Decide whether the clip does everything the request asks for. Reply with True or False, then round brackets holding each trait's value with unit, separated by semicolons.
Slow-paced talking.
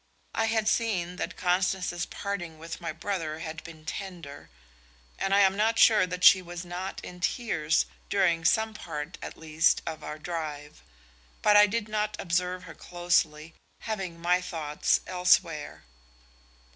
False (150 wpm)